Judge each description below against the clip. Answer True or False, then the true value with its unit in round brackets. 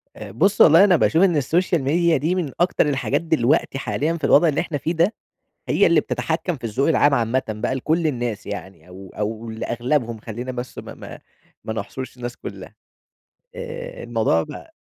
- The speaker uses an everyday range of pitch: False (6.2 semitones)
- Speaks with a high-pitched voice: False (140 Hz)